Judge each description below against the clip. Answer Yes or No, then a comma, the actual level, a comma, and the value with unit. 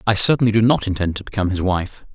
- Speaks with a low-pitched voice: Yes, low, 105 Hz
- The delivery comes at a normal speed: No, fast, 250 wpm